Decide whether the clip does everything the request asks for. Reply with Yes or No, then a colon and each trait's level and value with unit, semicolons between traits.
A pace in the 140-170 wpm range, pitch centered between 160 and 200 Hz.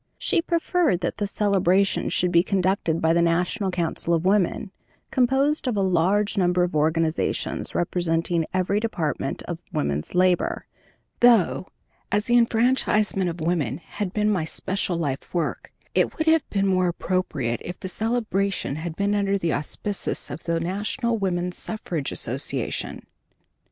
Yes: average, 150 wpm; medium, 185 Hz